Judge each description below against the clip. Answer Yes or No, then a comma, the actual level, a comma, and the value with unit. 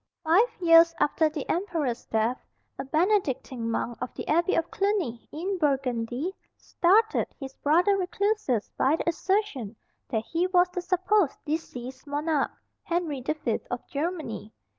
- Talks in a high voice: Yes, very high, 320 Hz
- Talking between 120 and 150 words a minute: Yes, average, 140 wpm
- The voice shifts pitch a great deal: Yes, wide, 5.8 semitones